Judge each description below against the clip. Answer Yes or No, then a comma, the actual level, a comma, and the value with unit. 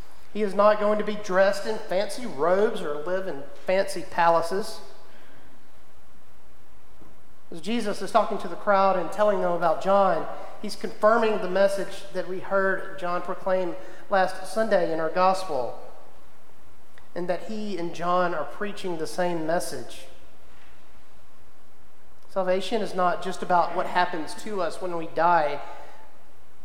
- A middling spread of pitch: Yes, average, 3.2 semitones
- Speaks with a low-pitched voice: No, medium, 185 Hz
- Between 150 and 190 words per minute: No, average, 140 wpm